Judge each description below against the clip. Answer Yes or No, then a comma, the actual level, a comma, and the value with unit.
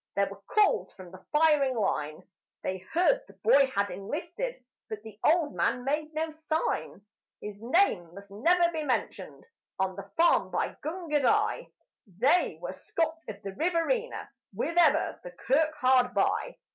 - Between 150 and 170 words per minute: Yes, average, 155 wpm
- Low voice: No, very high, 280 Hz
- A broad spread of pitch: Yes, wide, 8.7 semitones